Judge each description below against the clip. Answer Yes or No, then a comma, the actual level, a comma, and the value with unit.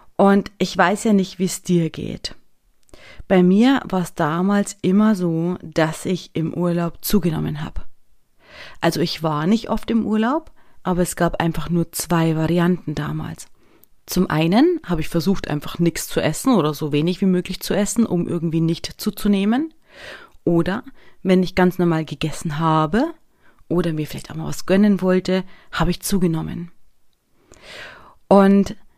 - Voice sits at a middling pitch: Yes, medium, 180 Hz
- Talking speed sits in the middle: Yes, average, 155 wpm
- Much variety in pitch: No, average, 3.3 semitones